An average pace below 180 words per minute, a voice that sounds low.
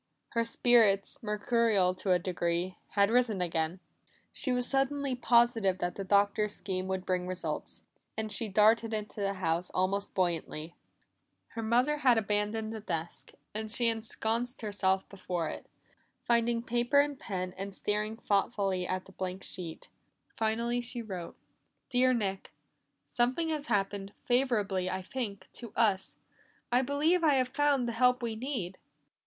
No: average, 150 wpm; high, 215 Hz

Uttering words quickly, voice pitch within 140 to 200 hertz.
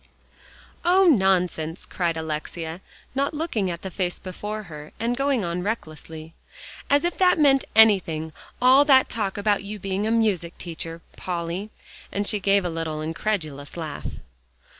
No: average, 150 wpm; high, 190 Hz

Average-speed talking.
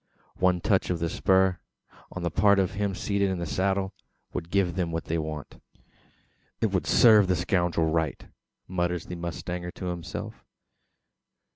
Yes: average, 160 wpm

